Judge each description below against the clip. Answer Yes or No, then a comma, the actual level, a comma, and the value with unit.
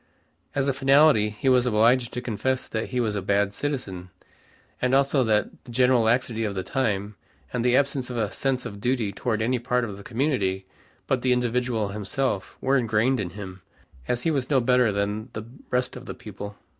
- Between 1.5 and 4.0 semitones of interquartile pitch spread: Yes, average, 3.6 semitones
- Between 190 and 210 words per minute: Yes, average, 200 wpm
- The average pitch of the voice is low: Yes, low, 120 Hz